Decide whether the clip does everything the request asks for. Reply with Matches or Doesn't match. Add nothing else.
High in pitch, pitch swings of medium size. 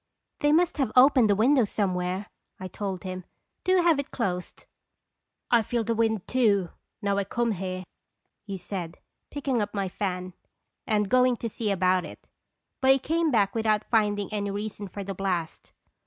Matches